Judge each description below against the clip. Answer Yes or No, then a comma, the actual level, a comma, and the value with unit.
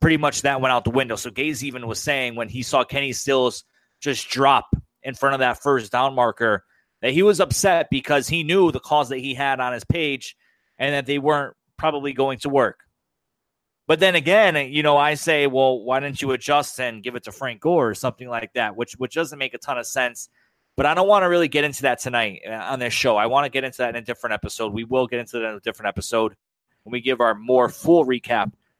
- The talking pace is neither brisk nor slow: No, fast, 245 wpm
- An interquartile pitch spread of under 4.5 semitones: Yes, average, 2.9 semitones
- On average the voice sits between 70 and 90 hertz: No, low, 135 Hz